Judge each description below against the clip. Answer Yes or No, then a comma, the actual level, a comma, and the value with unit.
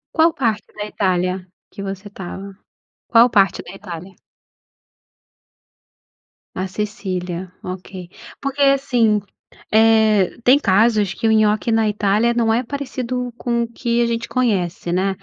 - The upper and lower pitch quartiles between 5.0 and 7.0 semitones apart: No, average, 3.7 semitones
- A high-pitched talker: Yes, high, 215 Hz